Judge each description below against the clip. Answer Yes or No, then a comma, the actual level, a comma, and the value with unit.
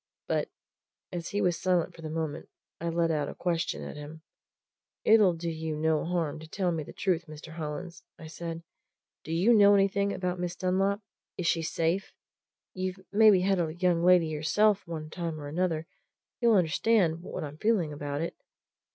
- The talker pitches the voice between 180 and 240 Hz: No, medium, 170 Hz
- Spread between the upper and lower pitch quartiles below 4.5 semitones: Yes, average, 2.7 semitones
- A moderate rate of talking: Yes, average, 180 wpm